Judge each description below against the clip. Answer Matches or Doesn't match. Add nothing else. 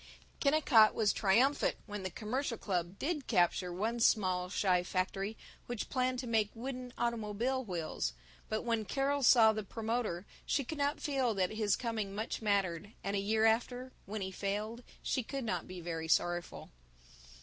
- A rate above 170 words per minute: Doesn't match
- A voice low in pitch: Doesn't match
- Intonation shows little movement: Doesn't match